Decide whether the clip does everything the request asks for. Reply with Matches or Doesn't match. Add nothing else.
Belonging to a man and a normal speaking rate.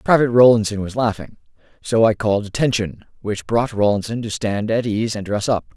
Matches